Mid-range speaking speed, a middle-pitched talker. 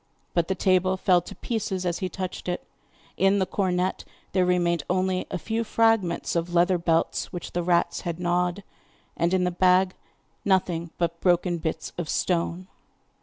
Yes: average, 170 wpm; medium, 180 Hz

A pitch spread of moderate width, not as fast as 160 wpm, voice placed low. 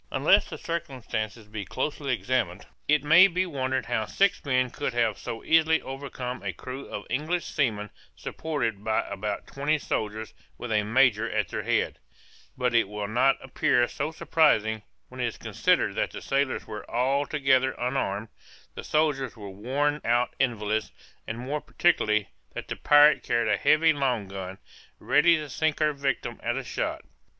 No: average, 5.0 semitones; average, 165 wpm; low, 130 Hz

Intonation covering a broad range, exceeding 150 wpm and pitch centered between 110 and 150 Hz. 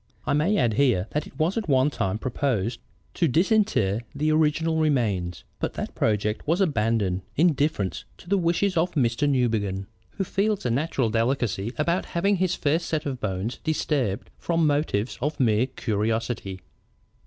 Yes: wide, 6.6 semitones; average, 165 wpm; low, 135 Hz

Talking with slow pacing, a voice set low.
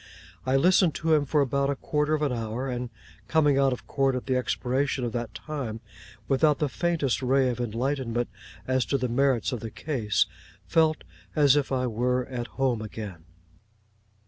No: average, 180 wpm; low, 130 Hz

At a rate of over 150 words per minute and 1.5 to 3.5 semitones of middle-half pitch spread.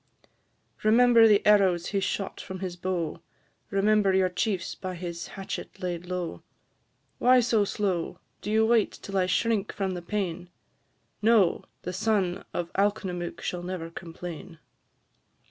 No: average, 140 wpm; average, 2.9 semitones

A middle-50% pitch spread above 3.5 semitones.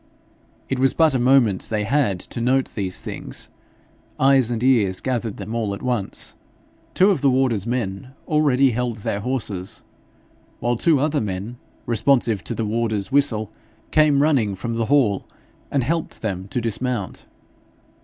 Yes: average, 4.2 semitones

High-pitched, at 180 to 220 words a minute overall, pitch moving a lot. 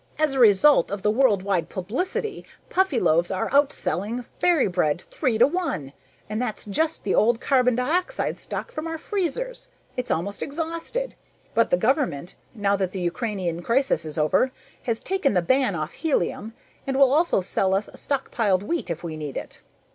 No: high, 230 Hz; average, 170 wpm; wide, 7.9 semitones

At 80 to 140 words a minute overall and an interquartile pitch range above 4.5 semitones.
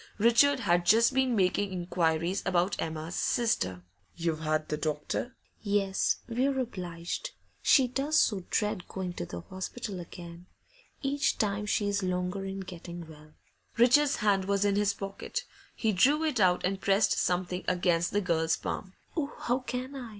No: average, 155 wpm; average, 5.1 semitones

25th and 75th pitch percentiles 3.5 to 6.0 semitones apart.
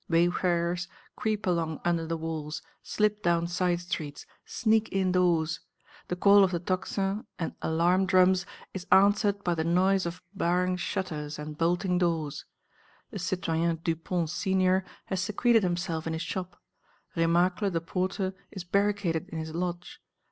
No: narrow, 2.4 semitones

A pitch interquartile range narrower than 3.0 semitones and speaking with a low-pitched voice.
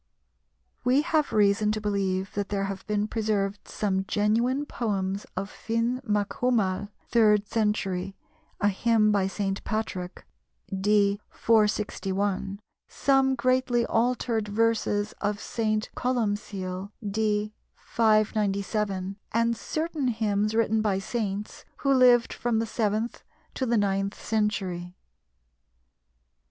No: narrow, 2.4 semitones; high, 210 Hz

